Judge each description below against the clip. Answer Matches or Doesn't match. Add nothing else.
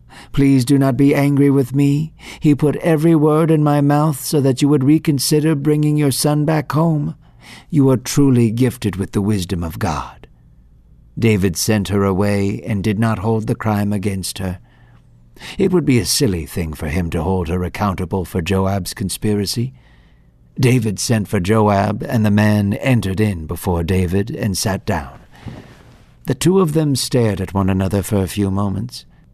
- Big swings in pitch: Matches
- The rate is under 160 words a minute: Doesn't match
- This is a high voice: Doesn't match